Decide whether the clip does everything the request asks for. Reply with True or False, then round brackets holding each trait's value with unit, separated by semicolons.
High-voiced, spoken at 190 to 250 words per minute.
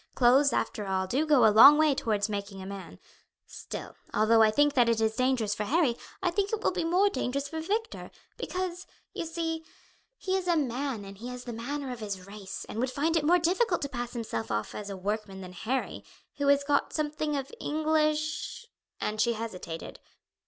True (260 Hz; 205 wpm)